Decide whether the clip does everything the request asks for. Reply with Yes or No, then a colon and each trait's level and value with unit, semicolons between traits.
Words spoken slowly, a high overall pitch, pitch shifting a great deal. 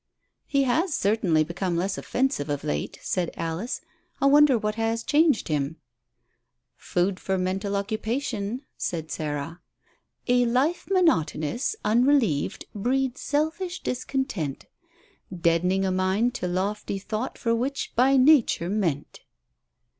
Yes: slow, 120 wpm; high, 210 Hz; wide, 6.9 semitones